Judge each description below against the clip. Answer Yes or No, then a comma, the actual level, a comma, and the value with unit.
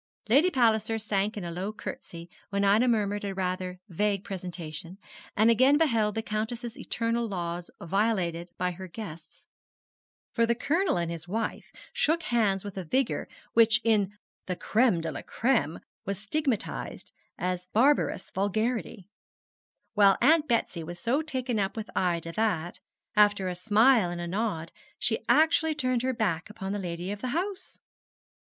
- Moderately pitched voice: No, high, 210 Hz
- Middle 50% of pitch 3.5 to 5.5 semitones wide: Yes, average, 4.5 semitones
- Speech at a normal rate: Yes, average, 160 wpm